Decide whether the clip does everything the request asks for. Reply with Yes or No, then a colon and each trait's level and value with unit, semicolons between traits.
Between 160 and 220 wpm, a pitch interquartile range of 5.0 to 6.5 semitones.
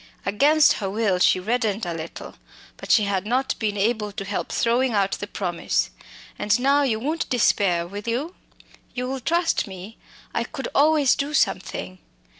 Yes: average, 165 wpm; average, 5.3 semitones